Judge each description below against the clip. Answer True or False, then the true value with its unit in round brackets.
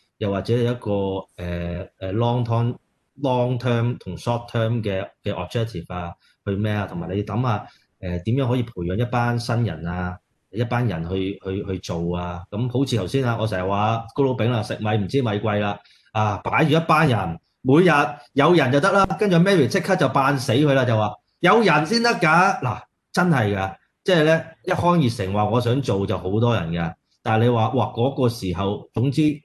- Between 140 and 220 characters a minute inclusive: False (330 characters per minute)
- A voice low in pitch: True (115 Hz)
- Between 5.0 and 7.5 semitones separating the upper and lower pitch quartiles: True (5.6 semitones)